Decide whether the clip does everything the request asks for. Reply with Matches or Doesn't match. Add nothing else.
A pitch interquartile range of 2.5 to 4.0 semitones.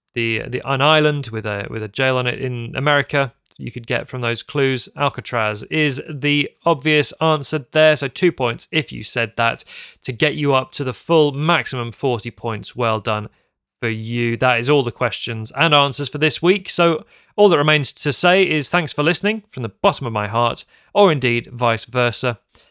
Doesn't match